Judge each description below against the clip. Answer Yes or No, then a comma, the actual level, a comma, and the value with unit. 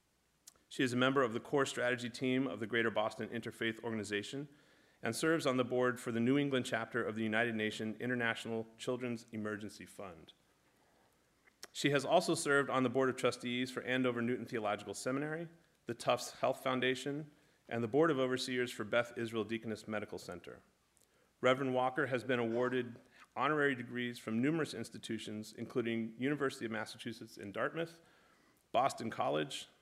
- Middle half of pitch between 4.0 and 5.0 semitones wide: No, average, 2.7 semitones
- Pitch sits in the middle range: No, low, 125 Hz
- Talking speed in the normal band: Yes, average, 160 wpm